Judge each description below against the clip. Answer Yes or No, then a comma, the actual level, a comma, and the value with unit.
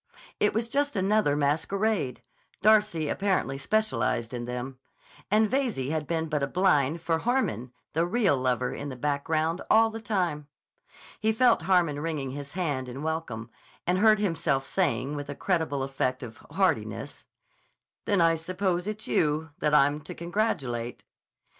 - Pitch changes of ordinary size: No, wide, 6.5 semitones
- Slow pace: No, average, 145 wpm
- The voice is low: No, medium, 160 Hz